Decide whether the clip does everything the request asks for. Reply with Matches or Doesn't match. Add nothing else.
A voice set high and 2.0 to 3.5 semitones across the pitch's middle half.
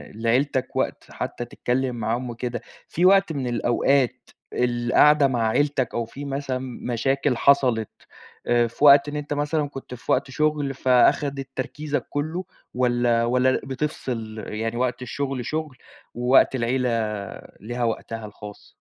Doesn't match